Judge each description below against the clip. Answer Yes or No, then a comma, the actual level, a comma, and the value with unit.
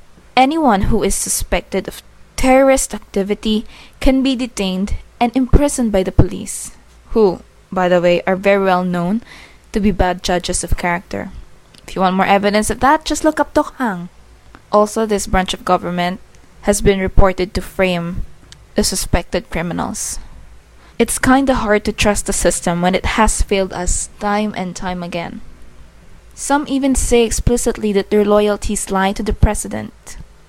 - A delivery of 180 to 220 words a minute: No, average, 160 wpm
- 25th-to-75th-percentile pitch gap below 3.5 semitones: No, average, 4.0 semitones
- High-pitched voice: Yes, high, 200 Hz